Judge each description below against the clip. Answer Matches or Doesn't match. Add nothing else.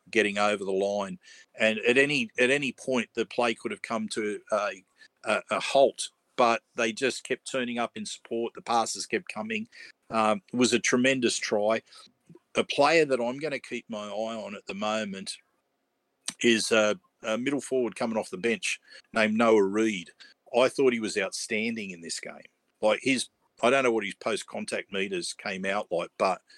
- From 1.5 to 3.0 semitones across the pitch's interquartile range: Matches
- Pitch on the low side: Matches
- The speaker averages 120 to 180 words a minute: Doesn't match